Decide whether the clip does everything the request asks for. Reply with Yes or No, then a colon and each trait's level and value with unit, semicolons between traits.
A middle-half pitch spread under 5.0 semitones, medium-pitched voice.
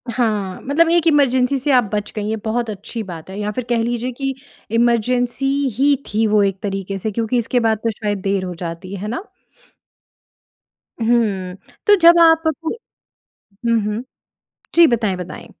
No: average, 4.1 semitones; high, 230 Hz